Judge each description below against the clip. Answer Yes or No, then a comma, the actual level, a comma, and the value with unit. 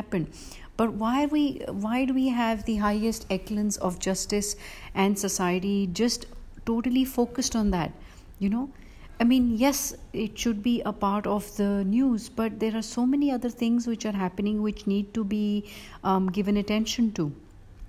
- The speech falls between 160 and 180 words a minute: Yes, average, 170 wpm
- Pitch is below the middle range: No, high, 215 Hz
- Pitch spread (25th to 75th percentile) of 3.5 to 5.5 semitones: No, average, 2.8 semitones